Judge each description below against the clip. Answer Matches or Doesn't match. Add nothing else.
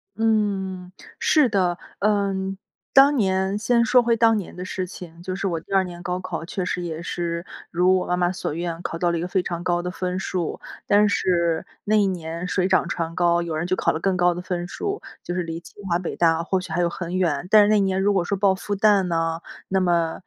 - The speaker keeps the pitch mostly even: Matches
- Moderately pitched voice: Matches